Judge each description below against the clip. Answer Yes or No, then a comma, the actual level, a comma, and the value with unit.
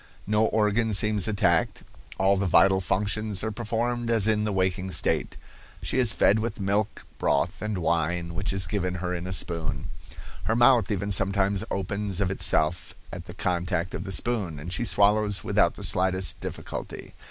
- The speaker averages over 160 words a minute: Yes, average, 175 wpm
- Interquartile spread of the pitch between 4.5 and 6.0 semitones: No, average, 2.9 semitones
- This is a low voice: Yes, low, 100 Hz